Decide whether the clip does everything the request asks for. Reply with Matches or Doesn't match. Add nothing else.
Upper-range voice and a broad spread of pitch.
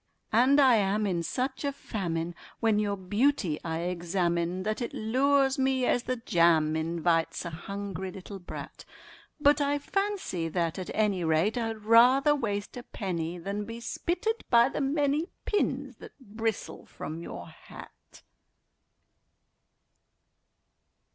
Matches